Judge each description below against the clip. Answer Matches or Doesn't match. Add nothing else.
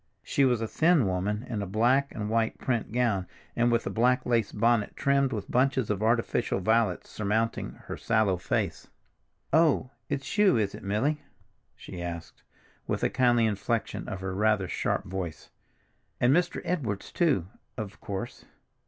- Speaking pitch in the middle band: Doesn't match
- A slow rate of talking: Doesn't match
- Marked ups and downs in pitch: Doesn't match